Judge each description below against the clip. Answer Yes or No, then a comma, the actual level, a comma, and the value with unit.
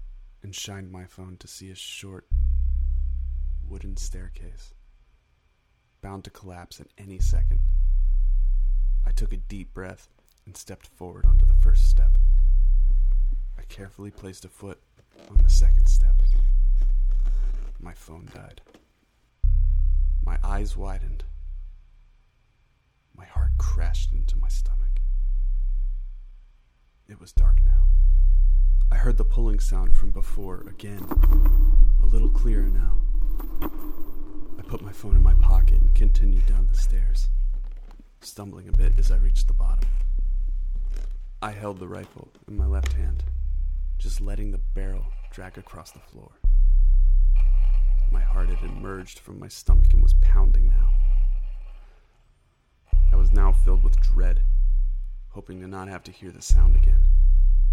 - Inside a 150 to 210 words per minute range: No, slow, 135 wpm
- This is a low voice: Yes, very low, 70 Hz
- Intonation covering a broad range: Yes, wide, 6.2 semitones